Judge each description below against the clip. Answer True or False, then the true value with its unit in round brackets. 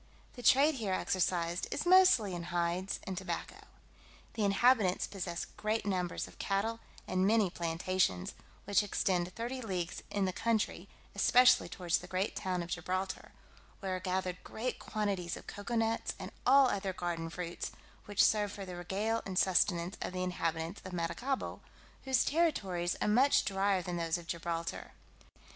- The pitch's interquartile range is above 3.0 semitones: True (3.6 semitones)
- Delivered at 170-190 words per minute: False (160 wpm)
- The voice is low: False (190 Hz)